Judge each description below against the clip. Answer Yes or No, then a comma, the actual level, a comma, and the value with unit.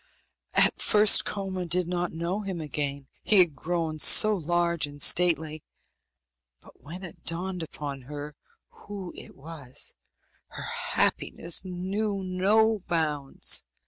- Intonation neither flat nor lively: Yes, average, 3.7 semitones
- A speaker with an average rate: No, slow, 125 wpm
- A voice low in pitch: No, medium, 175 Hz